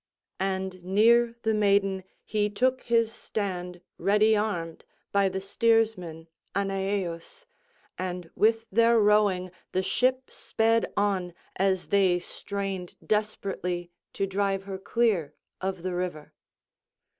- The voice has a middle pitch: No, high, 195 Hz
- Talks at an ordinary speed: No, slow, 115 wpm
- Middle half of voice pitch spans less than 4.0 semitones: Yes, average, 2.9 semitones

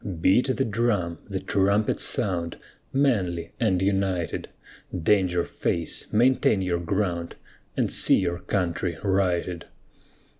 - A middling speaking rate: No, slow, 110 wpm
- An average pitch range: Yes, average, 3.2 semitones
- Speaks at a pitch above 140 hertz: No, very low, 95 Hz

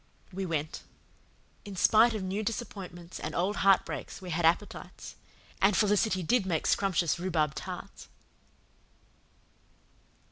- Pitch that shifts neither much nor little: Yes, average, 3.3 semitones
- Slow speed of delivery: Yes, slow, 115 wpm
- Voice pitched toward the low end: No, medium, 185 Hz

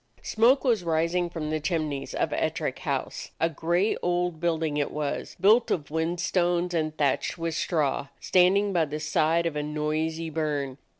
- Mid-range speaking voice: Yes, medium, 165 Hz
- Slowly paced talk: No, average, 170 wpm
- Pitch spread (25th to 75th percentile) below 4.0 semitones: Yes, narrow, 2.6 semitones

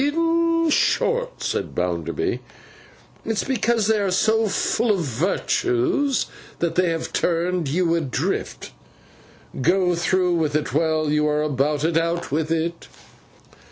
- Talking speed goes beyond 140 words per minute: No, slow, 135 wpm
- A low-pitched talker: No, medium, 170 Hz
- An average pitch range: No, wide, 6.1 semitones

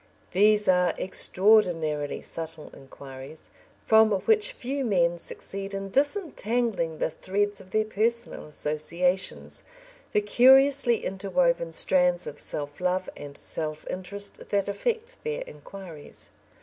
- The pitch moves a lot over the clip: Yes, wide, 5.7 semitones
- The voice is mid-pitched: No, high, 195 Hz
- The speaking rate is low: Yes, slow, 115 wpm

